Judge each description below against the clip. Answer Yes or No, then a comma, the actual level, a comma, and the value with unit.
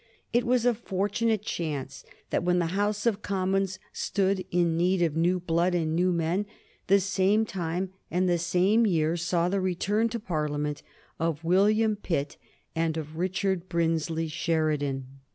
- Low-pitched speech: No, medium, 180 Hz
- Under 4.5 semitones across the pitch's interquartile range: Yes, average, 3.3 semitones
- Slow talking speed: No, average, 155 wpm